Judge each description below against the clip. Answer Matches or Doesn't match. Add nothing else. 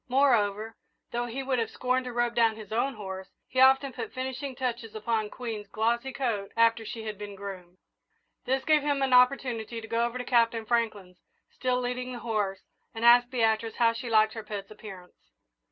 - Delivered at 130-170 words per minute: Doesn't match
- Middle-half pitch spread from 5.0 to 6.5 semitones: Doesn't match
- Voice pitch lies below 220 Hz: Doesn't match